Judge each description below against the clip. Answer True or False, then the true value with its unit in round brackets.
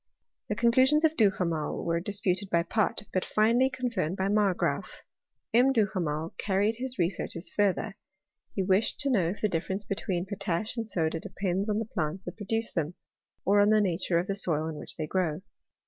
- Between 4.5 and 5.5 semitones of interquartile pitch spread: False (3.9 semitones)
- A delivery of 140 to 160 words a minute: False (180 wpm)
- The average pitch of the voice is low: False (195 Hz)